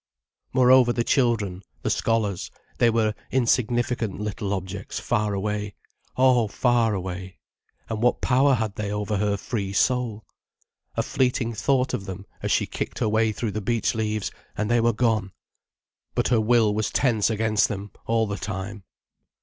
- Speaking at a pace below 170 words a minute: Yes, average, 160 wpm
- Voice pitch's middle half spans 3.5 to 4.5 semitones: No, average, 2.7 semitones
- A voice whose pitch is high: No, low, 110 Hz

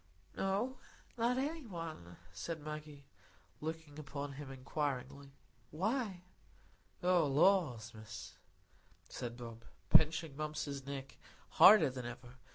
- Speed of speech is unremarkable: No, slow, 110 wpm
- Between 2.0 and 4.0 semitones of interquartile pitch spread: No, average, 5.2 semitones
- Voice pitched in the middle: Yes, medium, 150 Hz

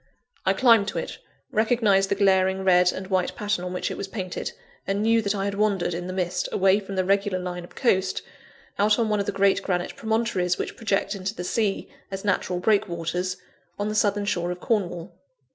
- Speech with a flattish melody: Yes, narrow, 2.3 semitones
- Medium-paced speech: No, fast, 210 wpm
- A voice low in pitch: No, high, 195 Hz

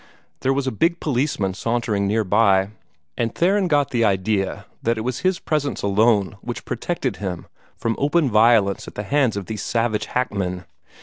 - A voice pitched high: No, low, 115 Hz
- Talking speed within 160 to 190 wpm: Yes, average, 175 wpm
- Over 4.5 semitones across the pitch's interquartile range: Yes, average, 5.1 semitones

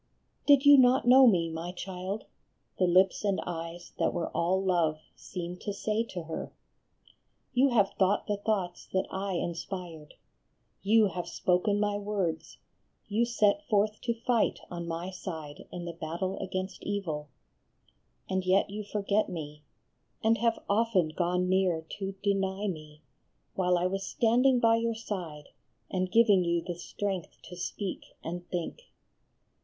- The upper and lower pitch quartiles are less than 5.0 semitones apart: Yes, average, 3.3 semitones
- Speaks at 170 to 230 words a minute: No, average, 155 wpm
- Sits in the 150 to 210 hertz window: Yes, high, 190 Hz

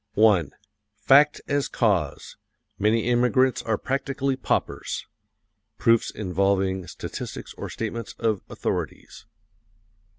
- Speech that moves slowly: Yes, slow, 90 wpm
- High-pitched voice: No, low, 115 Hz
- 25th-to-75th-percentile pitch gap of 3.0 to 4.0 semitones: No, average, 4.8 semitones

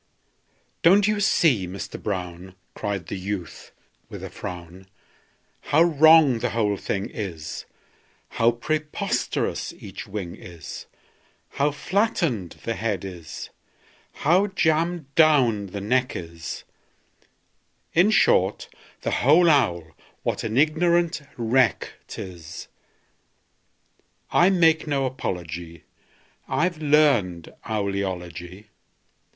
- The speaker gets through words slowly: Yes, slow, 105 wpm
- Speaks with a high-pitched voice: No, low, 115 Hz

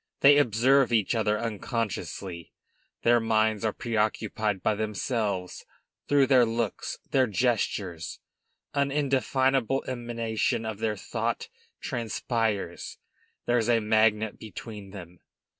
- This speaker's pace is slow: Yes, slow, 110 wpm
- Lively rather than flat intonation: No, narrow, 2.4 semitones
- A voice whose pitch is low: Yes, low, 110 Hz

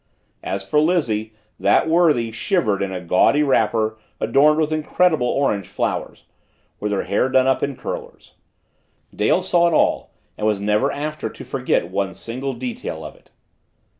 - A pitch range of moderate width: No, wide, 6.4 semitones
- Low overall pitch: Yes, low, 130 Hz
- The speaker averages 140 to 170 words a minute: Yes, average, 160 wpm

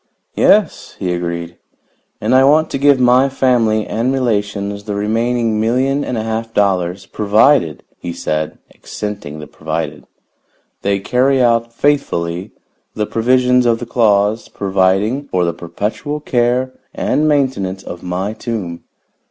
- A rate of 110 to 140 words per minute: Yes, slow, 135 wpm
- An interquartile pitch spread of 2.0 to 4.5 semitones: No, average, 4.9 semitones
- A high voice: No, low, 110 Hz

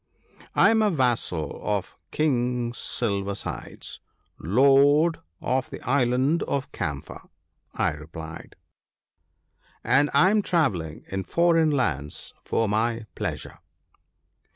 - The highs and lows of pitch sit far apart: Yes, wide, 6.8 semitones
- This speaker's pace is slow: Yes, slow, 110 wpm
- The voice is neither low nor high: No, low, 125 Hz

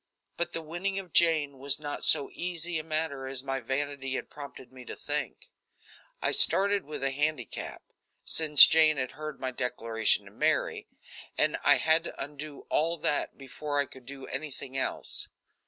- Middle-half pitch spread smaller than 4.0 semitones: Yes, average, 2.9 semitones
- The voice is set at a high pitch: No, medium, 145 Hz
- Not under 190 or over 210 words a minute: No, average, 170 wpm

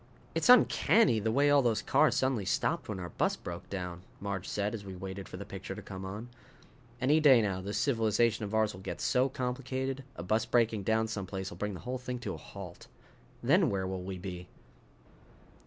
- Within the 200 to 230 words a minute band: Yes, fast, 205 wpm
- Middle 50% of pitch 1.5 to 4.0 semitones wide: No, average, 4.7 semitones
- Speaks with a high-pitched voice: No, low, 105 Hz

